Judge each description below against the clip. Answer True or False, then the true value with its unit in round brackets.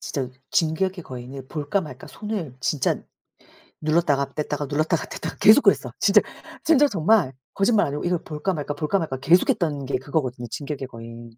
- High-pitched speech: False (150 Hz)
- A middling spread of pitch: True (4.7 semitones)